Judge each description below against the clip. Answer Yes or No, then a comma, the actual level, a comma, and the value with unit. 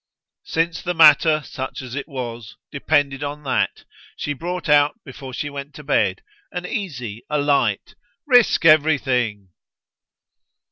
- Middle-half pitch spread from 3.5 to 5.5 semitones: No, average, 3.1 semitones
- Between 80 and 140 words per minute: Yes, slow, 135 wpm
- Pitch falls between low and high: Yes, medium, 145 Hz